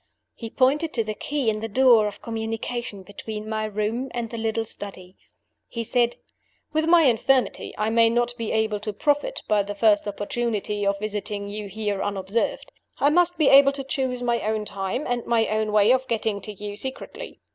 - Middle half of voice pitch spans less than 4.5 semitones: Yes, average, 3.1 semitones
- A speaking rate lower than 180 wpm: No, average, 190 wpm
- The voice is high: Yes, high, 225 Hz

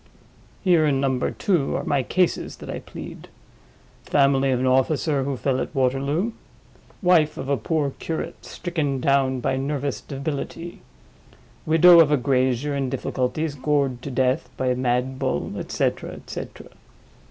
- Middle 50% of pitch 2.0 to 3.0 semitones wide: Yes, narrow, 2.6 semitones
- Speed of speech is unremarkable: Yes, average, 155 wpm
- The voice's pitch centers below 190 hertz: Yes, medium, 140 Hz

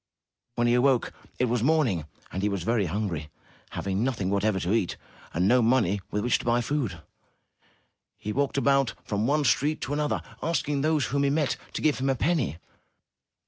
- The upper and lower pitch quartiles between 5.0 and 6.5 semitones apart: Yes, wide, 5.5 semitones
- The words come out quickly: No, average, 185 wpm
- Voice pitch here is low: Yes, low, 120 Hz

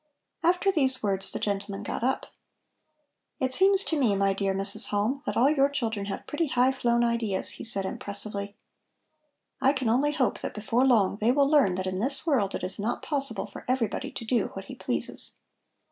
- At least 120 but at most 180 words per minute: No, average, 195 wpm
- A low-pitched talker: No, high, 235 Hz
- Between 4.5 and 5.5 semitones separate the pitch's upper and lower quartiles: Yes, average, 5.1 semitones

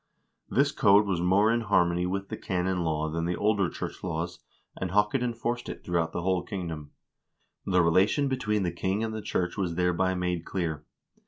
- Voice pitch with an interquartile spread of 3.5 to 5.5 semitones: No, average, 3.1 semitones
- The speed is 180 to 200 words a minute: Yes, average, 190 wpm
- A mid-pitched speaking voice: No, very low, 90 Hz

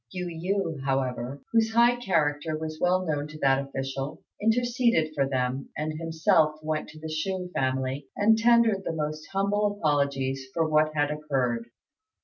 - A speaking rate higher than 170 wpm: No, average, 155 wpm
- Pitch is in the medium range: Yes, medium, 155 Hz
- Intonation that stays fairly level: No, wide, 5.5 semitones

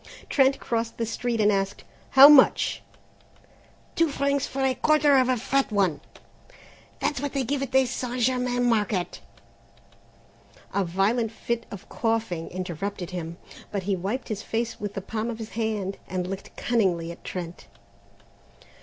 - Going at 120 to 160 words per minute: Yes, average, 155 wpm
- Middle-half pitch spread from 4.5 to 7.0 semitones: Yes, average, 4.8 semitones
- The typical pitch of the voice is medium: No, high, 225 Hz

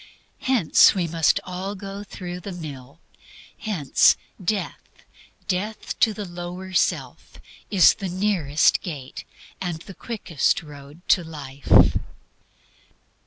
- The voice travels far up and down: No, average, 4.0 semitones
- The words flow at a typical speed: No, slow, 115 wpm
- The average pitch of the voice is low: No, medium, 180 Hz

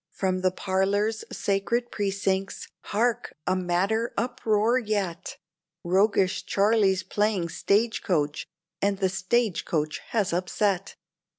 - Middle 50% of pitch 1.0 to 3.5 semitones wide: Yes, average, 2.7 semitones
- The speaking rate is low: Yes, slow, 115 wpm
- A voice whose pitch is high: Yes, high, 195 Hz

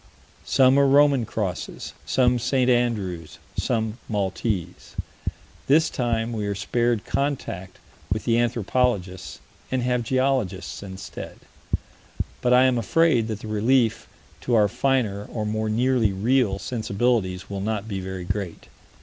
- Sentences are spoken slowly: Yes, slow, 130 wpm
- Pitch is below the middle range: Yes, low, 115 Hz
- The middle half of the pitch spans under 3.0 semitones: No, average, 4.0 semitones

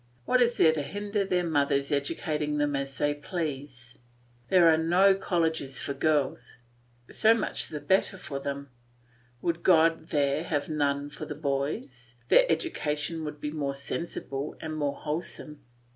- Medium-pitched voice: Yes, medium, 150 Hz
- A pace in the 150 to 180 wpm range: Yes, average, 155 wpm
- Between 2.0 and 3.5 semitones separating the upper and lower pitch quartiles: Yes, average, 2.9 semitones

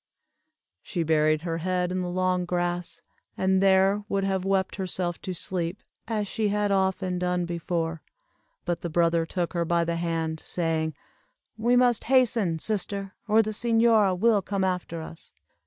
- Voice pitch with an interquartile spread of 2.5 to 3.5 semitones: Yes, average, 2.8 semitones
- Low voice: No, medium, 185 Hz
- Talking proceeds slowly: No, average, 160 wpm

